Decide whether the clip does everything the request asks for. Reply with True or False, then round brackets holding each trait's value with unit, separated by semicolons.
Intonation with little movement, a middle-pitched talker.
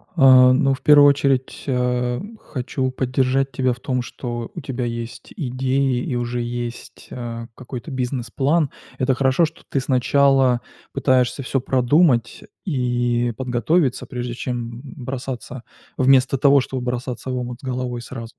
False (1.7 semitones; 125 Hz)